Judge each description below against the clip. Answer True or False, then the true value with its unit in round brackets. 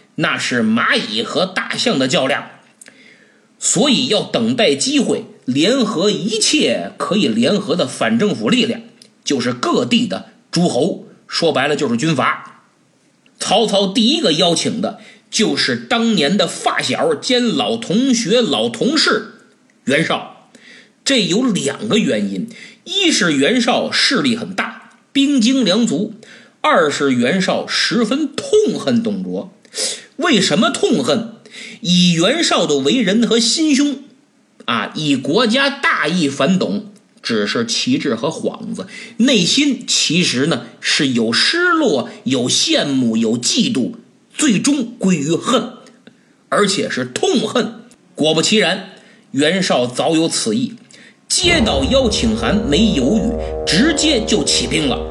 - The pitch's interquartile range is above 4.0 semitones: False (3.2 semitones)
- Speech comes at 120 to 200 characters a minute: True (190 characters per minute)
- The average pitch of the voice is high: True (230 Hz)